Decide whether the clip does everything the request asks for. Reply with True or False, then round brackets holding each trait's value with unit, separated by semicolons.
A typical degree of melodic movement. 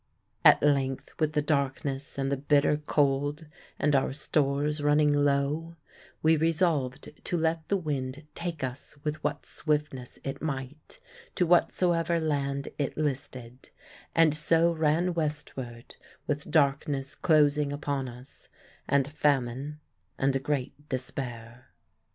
False (2.3 semitones)